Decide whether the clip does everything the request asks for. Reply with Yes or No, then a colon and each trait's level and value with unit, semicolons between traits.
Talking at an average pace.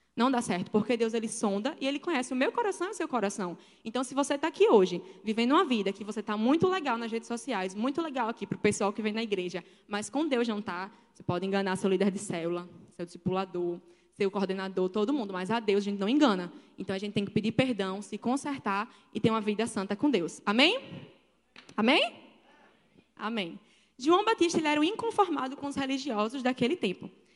No: fast, 220 wpm